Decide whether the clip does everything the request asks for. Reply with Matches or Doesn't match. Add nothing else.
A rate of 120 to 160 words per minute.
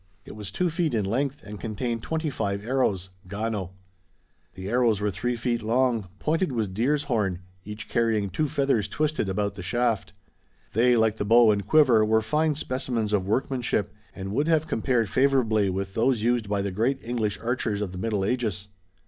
Doesn't match